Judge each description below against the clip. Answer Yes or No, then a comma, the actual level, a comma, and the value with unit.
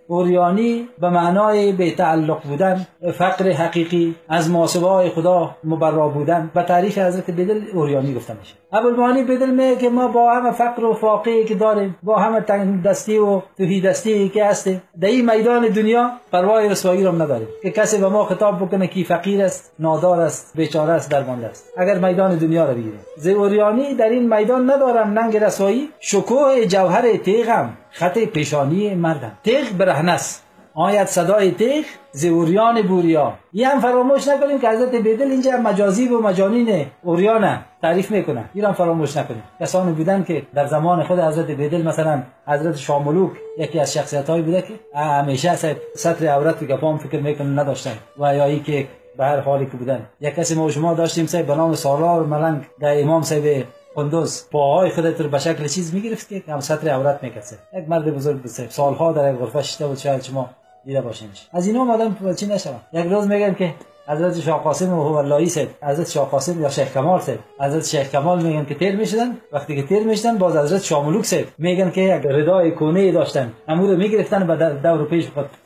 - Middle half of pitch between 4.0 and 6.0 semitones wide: Yes, wide, 5.4 semitones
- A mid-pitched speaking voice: Yes, medium, 175 Hz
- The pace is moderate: No, fast, 180 wpm